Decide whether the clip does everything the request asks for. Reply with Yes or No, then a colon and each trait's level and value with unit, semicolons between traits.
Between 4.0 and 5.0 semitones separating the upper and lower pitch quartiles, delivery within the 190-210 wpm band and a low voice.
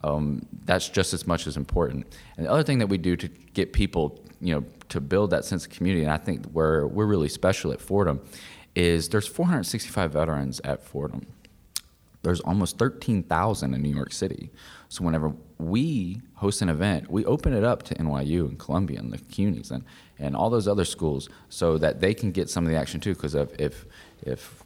Yes: average, 4.6 semitones; average, 200 wpm; very low, 85 Hz